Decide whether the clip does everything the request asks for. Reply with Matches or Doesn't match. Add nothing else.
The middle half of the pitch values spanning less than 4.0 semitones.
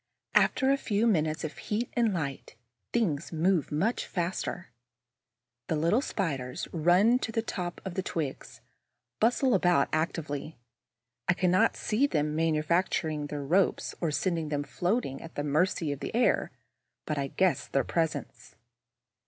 Doesn't match